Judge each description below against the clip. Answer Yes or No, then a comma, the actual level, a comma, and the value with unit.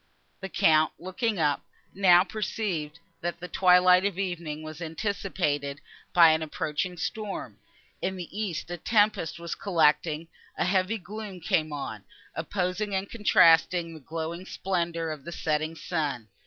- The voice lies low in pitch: No, medium, 175 Hz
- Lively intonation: No, average, 3.2 semitones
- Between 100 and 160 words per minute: Yes, average, 140 wpm